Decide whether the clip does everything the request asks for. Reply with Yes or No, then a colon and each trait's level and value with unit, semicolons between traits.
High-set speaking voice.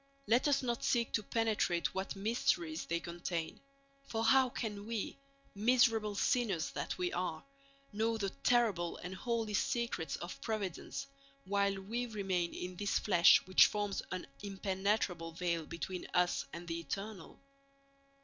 Yes: high, 200 Hz